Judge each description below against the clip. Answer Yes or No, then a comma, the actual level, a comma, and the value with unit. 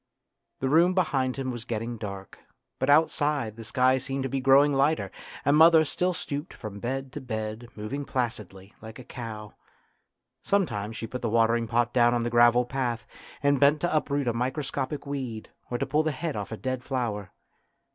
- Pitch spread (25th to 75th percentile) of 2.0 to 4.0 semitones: Yes, average, 3.7 semitones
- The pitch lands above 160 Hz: No, low, 125 Hz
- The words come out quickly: No, average, 190 wpm